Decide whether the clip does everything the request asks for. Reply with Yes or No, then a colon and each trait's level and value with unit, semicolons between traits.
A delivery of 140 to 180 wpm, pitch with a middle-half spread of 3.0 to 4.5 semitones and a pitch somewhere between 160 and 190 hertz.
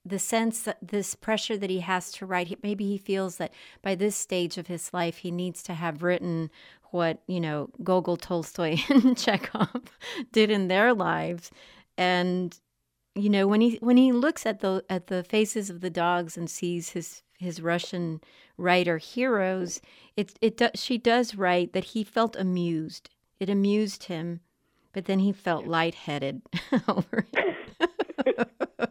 Yes: average, 165 wpm; average, 3.6 semitones; medium, 185 Hz